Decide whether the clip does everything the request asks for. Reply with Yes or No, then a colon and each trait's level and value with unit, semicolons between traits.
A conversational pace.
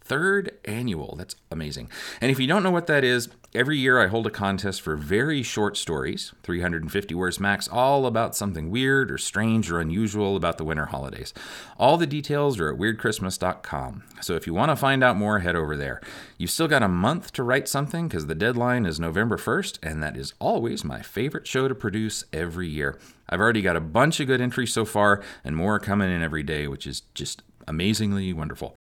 No: fast, 210 wpm